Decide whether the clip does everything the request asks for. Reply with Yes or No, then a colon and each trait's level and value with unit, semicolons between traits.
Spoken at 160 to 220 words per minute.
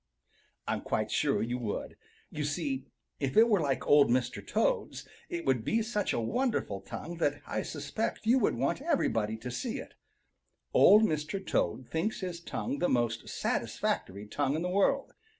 Yes: average, 170 wpm